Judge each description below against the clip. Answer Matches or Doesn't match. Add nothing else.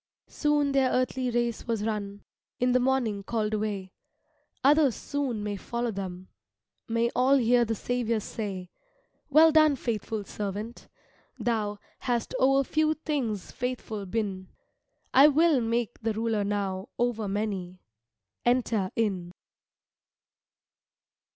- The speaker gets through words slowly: Matches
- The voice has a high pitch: Matches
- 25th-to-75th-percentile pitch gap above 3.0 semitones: Matches